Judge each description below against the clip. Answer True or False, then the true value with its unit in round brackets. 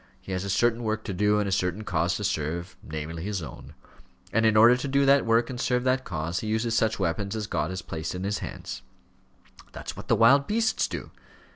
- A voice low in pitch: True (105 Hz)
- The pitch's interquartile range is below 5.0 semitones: True (4.5 semitones)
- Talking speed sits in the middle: False (230 wpm)